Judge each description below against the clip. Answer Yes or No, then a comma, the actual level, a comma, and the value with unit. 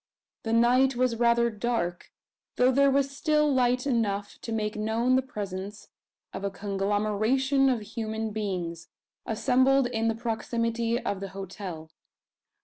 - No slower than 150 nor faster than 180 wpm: No, average, 140 wpm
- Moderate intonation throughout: Yes, average, 3.6 semitones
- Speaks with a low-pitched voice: No, high, 225 Hz